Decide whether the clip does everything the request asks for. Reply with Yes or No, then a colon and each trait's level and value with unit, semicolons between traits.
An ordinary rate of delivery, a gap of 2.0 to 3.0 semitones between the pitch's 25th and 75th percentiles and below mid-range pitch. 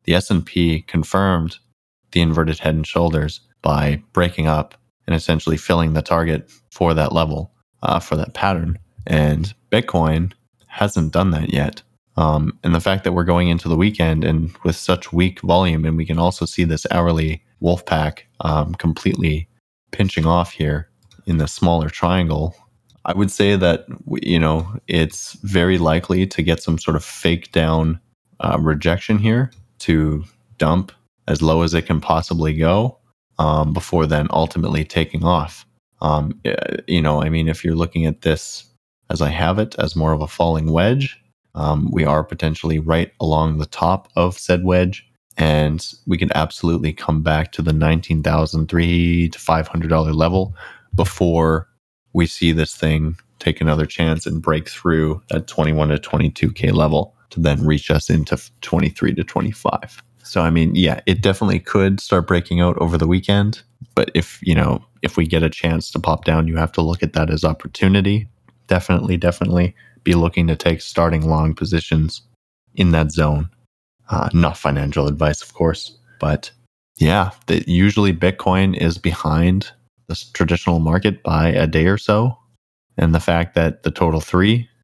Yes: average, 165 wpm; narrow, 2.6 semitones; very low, 85 Hz